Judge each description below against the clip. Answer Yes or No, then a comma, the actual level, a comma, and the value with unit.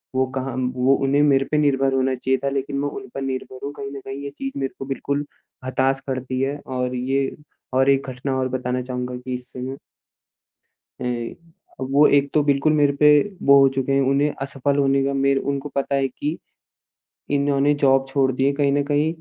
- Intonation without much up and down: Yes, narrow, 1.3 semitones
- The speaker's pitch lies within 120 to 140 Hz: Yes, low, 135 Hz